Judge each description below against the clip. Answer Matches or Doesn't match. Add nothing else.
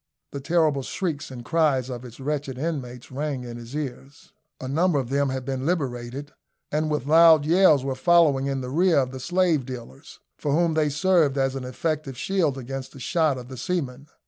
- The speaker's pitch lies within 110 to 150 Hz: Matches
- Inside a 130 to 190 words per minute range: Doesn't match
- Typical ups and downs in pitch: Matches